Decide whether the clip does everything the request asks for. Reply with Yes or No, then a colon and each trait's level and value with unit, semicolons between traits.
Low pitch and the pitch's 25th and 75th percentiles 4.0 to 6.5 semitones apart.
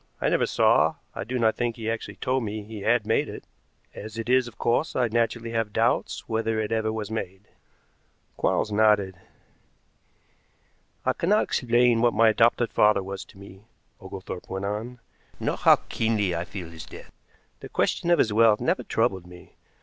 No: low, 110 Hz; narrow, 2.4 semitones